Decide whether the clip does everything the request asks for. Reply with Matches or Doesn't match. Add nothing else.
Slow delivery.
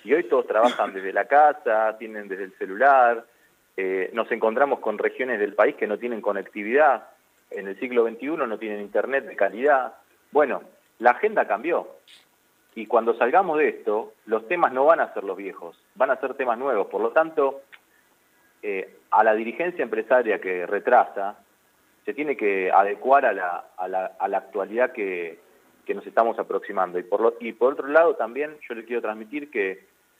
Doesn't match